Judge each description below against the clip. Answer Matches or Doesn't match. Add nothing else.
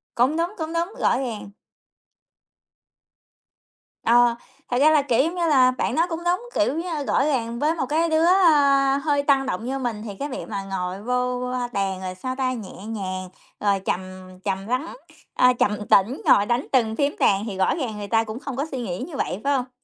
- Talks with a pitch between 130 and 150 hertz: Doesn't match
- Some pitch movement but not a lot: Doesn't match